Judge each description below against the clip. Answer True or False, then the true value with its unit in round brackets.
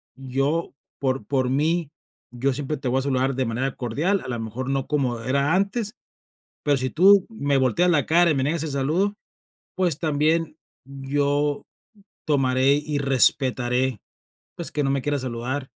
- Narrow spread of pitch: False (3.0 semitones)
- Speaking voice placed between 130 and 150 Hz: True (140 Hz)